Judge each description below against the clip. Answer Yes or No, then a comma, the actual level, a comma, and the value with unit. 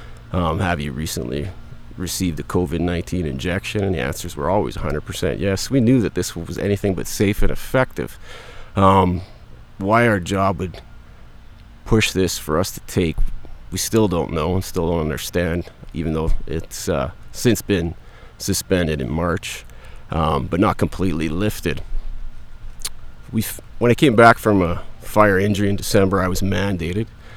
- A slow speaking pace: No, average, 160 wpm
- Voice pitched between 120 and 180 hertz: No, very low, 95 Hz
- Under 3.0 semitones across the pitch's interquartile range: No, average, 3.6 semitones